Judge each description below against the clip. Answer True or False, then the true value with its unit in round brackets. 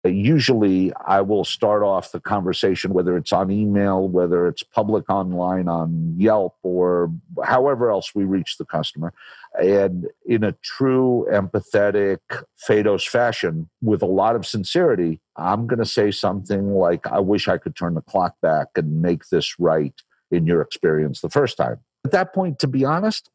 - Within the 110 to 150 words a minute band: False (170 wpm)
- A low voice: True (95 Hz)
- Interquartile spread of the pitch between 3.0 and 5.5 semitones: True (3.3 semitones)